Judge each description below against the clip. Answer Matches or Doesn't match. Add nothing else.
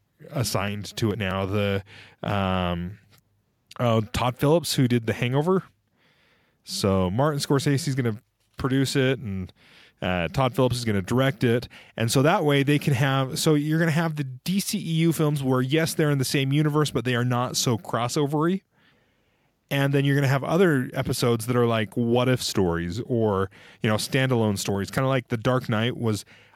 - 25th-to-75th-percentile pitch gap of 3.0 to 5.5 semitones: Matches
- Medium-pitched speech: Doesn't match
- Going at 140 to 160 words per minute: Doesn't match